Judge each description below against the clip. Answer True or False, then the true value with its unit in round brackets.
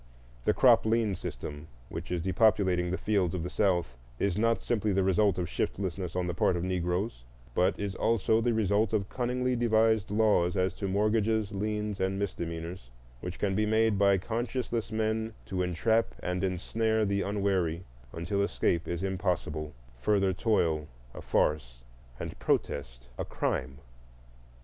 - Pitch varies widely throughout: False (3.7 semitones)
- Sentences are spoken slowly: False (155 wpm)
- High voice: False (100 Hz)